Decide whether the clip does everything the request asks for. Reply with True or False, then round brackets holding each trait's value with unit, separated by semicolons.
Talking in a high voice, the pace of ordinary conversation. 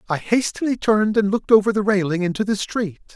False (205 Hz; 210 wpm)